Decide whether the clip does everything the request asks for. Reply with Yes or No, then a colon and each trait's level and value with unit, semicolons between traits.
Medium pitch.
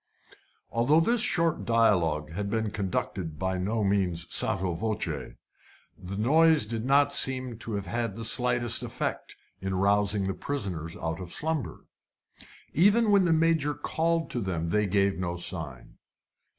No: low, 105 Hz